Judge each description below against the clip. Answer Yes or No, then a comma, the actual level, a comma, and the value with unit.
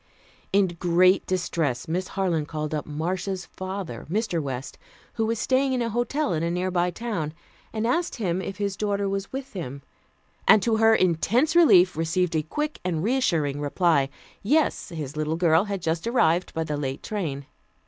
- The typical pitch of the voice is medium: Yes, medium, 180 Hz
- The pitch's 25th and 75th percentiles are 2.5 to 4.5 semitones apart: No, average, 5.1 semitones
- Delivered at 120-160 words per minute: No, average, 175 wpm